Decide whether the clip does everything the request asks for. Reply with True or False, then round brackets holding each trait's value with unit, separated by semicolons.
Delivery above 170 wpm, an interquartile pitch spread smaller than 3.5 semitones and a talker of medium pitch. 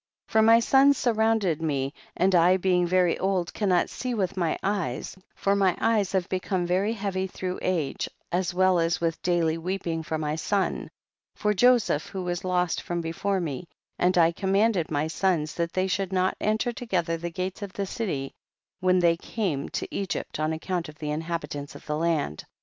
True (190 wpm; 2.9 semitones; 180 Hz)